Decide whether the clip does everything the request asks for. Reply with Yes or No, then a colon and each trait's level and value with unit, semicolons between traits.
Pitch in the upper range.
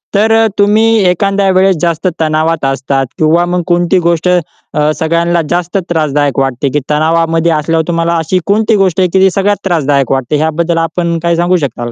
No: medium, 165 Hz